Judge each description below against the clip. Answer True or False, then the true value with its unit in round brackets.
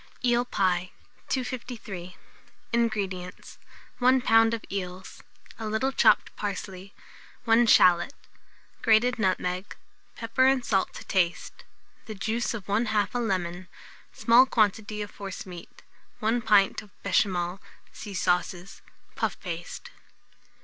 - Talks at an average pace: False (115 wpm)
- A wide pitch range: False (3.8 semitones)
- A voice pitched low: False (205 Hz)